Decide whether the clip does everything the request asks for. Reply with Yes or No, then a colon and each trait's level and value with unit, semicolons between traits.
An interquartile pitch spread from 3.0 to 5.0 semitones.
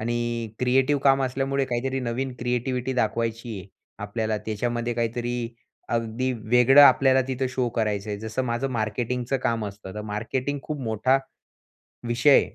No: narrow, 2.6 semitones